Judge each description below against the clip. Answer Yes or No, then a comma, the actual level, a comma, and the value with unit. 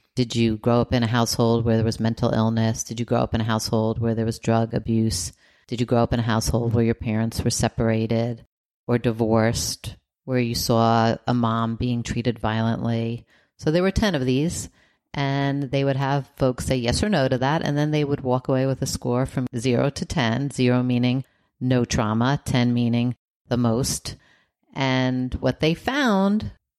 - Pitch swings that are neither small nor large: No, narrow, 2.3 semitones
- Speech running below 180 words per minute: No, average, 195 wpm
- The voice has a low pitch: Yes, low, 120 Hz